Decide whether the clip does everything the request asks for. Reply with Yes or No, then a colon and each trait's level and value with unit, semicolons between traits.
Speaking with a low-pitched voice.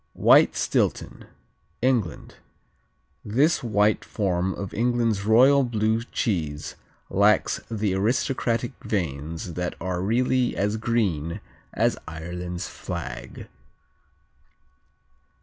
Yes: low, 105 Hz